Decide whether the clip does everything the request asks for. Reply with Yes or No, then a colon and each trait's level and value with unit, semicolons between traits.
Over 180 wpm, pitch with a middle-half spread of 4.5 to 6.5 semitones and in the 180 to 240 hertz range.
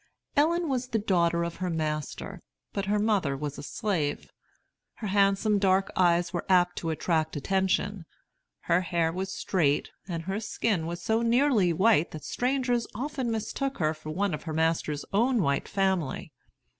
No: average, 165 wpm; average, 4.9 semitones; high, 190 Hz